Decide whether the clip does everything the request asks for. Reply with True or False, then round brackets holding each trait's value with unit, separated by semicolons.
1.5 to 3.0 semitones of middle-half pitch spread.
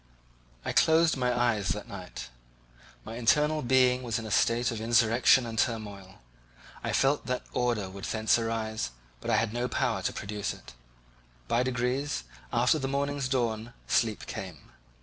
True (2.7 semitones)